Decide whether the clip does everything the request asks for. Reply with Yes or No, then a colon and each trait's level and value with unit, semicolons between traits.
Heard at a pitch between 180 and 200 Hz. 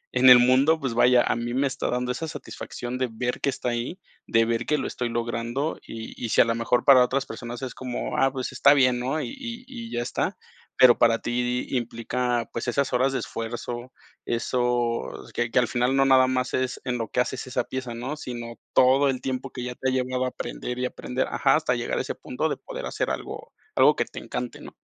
No: low, 125 Hz